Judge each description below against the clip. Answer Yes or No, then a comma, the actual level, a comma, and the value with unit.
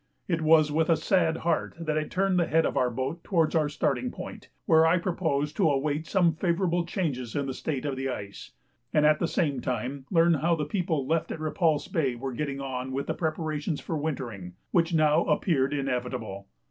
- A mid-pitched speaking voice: Yes, medium, 155 Hz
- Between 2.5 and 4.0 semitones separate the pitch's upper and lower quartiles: Yes, average, 3.5 semitones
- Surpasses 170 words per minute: Yes, average, 200 wpm